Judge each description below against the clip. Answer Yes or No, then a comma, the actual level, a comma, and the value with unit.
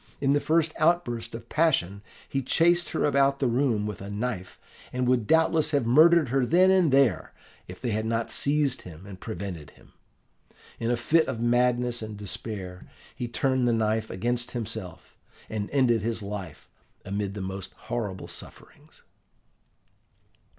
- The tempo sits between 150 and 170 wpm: Yes, average, 160 wpm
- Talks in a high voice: No, low, 120 Hz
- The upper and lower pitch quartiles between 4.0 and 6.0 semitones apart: Yes, average, 5.0 semitones